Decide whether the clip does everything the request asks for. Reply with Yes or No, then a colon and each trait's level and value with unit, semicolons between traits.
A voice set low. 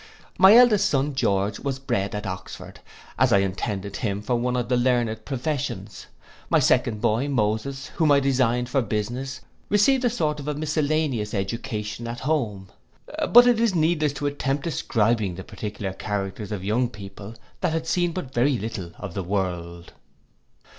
Yes: low, 120 Hz